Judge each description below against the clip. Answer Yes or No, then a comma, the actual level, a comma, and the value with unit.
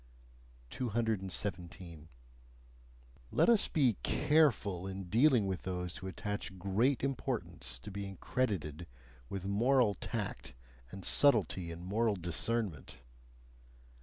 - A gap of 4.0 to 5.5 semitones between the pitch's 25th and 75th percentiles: Yes, average, 4.6 semitones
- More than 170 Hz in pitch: No, low, 100 Hz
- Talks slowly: Yes, slow, 105 wpm